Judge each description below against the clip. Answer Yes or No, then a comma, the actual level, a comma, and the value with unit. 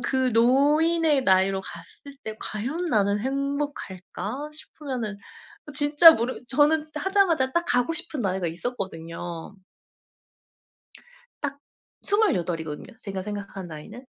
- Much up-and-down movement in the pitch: Yes, wide, 7.3 semitones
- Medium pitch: No, very high, 255 Hz